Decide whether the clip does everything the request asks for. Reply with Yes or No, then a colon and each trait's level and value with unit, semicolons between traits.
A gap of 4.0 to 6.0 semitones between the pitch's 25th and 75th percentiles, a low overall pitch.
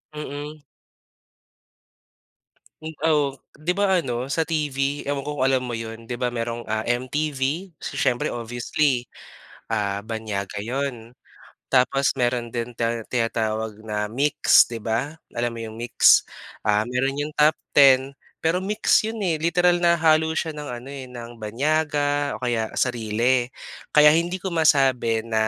Yes: average, 4.4 semitones; low, 130 Hz